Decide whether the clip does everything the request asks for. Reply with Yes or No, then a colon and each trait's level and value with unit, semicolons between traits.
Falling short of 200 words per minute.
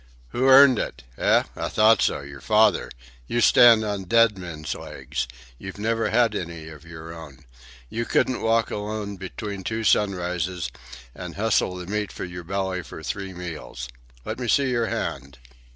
Yes: average, 170 wpm